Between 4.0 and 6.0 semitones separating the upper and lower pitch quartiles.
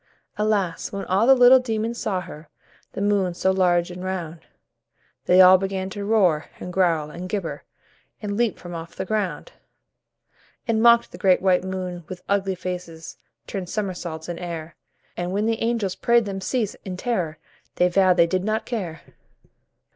No: average, 2.9 semitones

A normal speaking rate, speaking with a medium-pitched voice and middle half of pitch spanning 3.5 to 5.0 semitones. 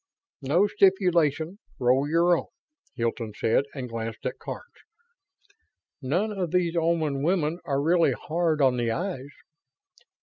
No: slow, 130 wpm; medium, 155 Hz; average, 4.7 semitones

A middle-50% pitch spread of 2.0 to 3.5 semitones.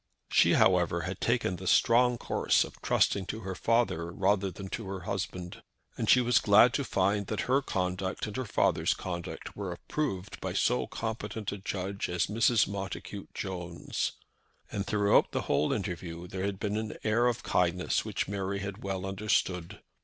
Yes: average, 2.9 semitones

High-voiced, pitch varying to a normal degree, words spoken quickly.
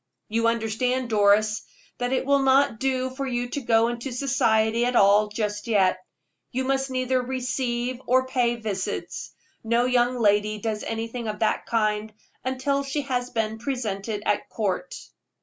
No: high, 240 Hz; average, 3.1 semitones; average, 155 wpm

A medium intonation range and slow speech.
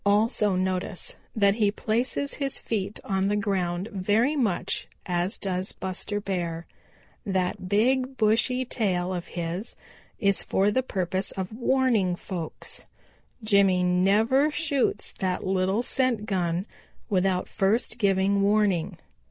Yes: average, 3.0 semitones; slow, 125 wpm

